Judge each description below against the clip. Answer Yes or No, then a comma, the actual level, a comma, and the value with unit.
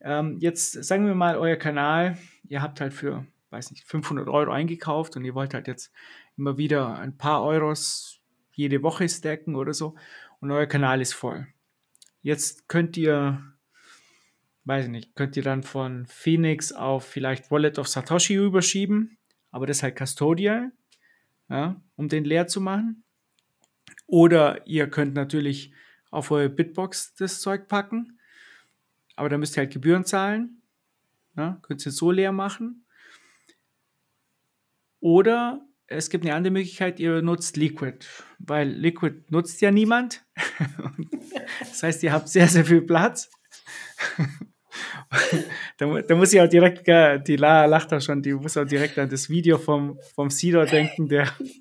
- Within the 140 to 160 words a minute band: Yes, average, 150 wpm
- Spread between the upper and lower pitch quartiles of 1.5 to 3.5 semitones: No, average, 4.0 semitones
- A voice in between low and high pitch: Yes, medium, 155 Hz